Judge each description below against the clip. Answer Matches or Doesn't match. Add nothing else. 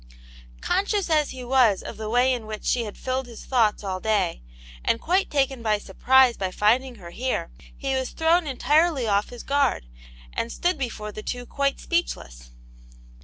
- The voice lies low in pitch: Doesn't match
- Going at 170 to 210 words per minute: Matches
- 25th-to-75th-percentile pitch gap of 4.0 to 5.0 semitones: Matches